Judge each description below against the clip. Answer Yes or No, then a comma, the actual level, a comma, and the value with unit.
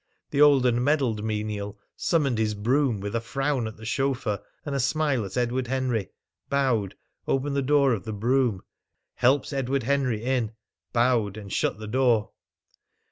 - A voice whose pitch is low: Yes, low, 125 Hz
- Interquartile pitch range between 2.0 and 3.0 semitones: No, average, 3.9 semitones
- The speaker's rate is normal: Yes, average, 165 wpm